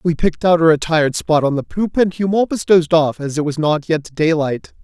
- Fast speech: Yes, fast, 235 wpm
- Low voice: No, medium, 165 Hz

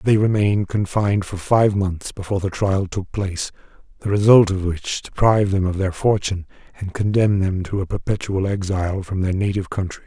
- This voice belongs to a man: Yes, male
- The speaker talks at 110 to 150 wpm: No, average, 185 wpm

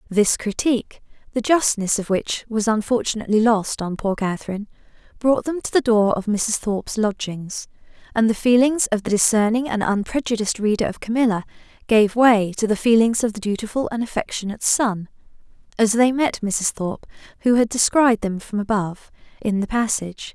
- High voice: Yes, high, 220 Hz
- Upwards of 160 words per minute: Yes, average, 170 wpm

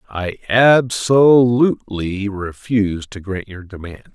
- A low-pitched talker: Yes, low, 105 Hz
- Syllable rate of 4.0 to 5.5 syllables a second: No, 3.6 syllables/s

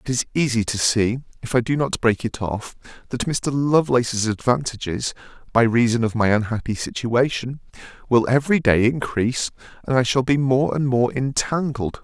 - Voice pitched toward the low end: Yes, low, 125 Hz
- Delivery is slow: No, average, 170 wpm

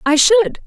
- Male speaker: No, female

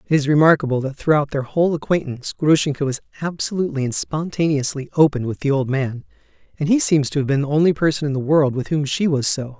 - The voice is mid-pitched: Yes, medium, 145 Hz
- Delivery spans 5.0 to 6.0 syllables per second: No, 6.3 syllables/s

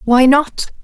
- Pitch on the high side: Yes, very high, 265 Hz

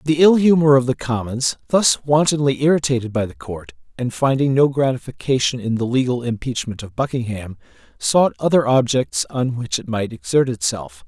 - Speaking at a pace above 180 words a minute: No, average, 170 wpm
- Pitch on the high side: No, low, 130 Hz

